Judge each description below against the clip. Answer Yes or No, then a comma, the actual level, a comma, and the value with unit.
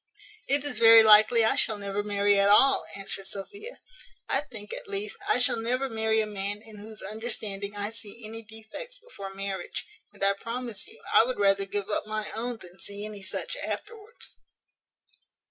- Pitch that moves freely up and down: No, narrow, 2.5 semitones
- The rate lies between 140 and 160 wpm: No, average, 180 wpm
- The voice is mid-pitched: No, high, 215 Hz